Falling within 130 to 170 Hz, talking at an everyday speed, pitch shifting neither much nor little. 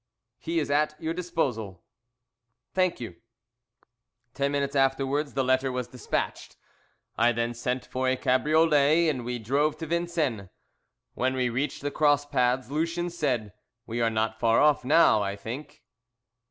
Yes: low, 135 Hz; average, 150 wpm; average, 4.0 semitones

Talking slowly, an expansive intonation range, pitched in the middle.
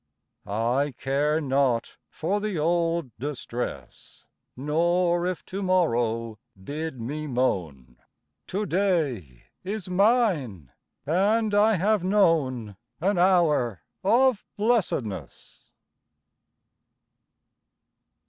Yes: slow, 85 wpm; wide, 7.7 semitones; medium, 160 Hz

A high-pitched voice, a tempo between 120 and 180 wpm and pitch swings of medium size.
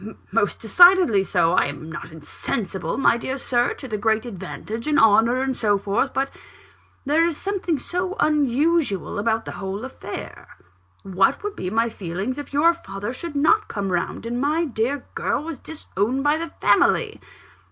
No: high, 240 Hz; average, 170 wpm; wide, 6.8 semitones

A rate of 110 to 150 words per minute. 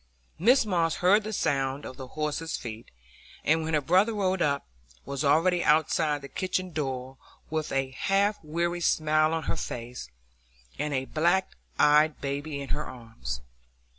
No: average, 160 wpm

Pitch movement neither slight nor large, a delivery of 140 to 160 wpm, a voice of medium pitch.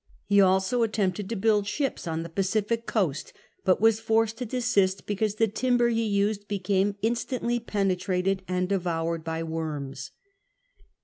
No: average, 3.6 semitones; average, 145 wpm; high, 200 Hz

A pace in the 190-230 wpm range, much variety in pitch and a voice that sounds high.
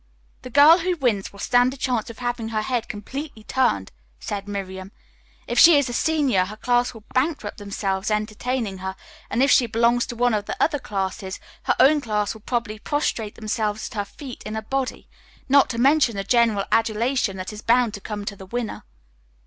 No: average, 200 wpm; average, 3.6 semitones; high, 225 Hz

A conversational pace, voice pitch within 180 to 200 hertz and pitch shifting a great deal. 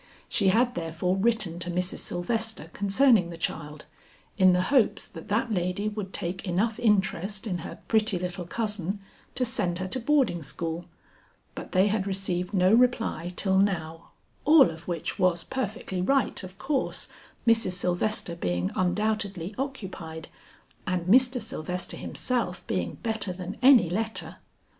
No: average, 150 wpm; high, 190 Hz; average, 4.0 semitones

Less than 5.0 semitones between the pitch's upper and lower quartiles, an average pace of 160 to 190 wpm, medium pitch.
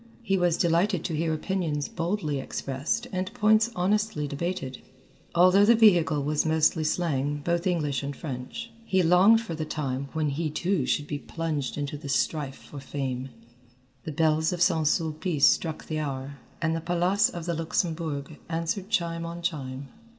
Yes: average, 3.5 semitones; average, 165 wpm; medium, 160 Hz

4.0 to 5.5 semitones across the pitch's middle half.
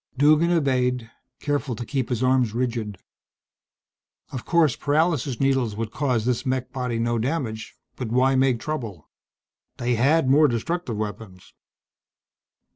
No: average, 3.6 semitones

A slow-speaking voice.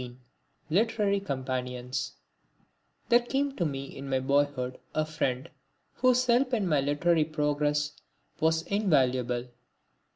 Yes: slow, 120 wpm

